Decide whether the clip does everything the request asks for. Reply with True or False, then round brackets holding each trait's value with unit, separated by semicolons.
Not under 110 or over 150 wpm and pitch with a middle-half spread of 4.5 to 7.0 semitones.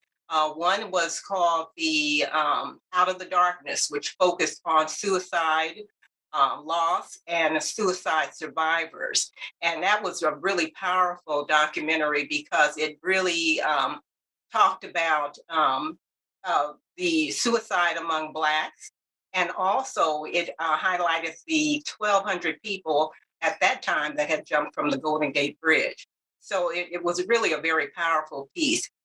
False (135 wpm; 3.6 semitones)